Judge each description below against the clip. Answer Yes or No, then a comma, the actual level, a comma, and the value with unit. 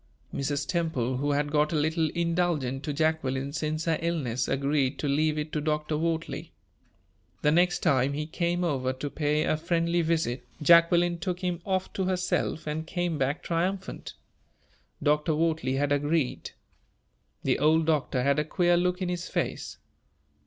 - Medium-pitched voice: Yes, medium, 155 Hz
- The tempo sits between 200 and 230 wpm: No, average, 160 wpm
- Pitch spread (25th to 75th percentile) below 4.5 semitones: Yes, average, 2.9 semitones